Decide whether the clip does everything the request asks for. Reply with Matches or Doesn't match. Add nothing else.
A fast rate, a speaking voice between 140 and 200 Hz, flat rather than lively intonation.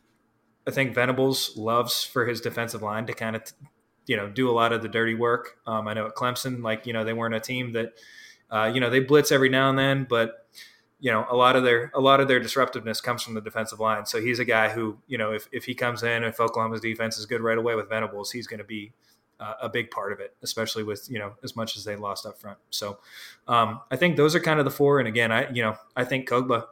Doesn't match